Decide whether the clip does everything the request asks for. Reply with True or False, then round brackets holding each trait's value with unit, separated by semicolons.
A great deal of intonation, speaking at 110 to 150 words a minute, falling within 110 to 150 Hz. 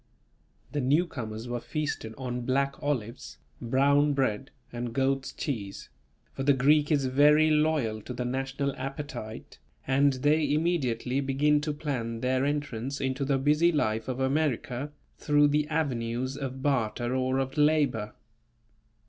False (2.9 semitones; 140 wpm; 135 Hz)